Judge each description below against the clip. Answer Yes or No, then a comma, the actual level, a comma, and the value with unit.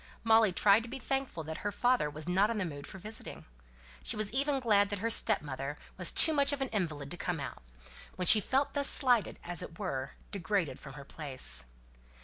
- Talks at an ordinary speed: No, fast, 215 wpm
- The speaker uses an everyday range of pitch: No, wide, 7.1 semitones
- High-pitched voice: Yes, high, 200 Hz